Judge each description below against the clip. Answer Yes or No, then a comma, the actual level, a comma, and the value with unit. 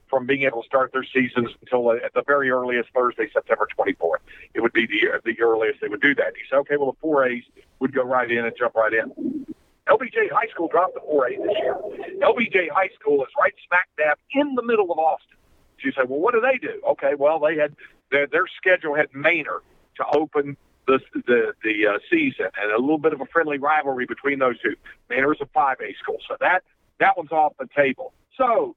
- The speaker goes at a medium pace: No, fast, 225 wpm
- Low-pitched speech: No, medium, 155 Hz